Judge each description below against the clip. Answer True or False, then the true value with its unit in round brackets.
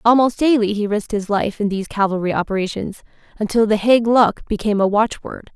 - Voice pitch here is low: False (215 Hz)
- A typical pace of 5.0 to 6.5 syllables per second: True (5.9 syllables/s)